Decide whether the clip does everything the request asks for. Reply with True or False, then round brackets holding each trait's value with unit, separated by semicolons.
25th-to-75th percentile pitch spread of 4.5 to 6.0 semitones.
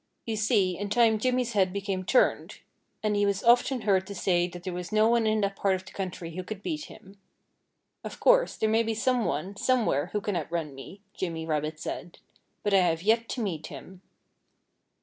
False (3.7 semitones)